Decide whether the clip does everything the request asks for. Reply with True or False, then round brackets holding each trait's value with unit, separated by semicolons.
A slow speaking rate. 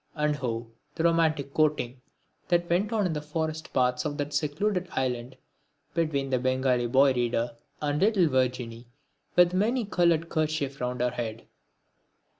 False (155 wpm)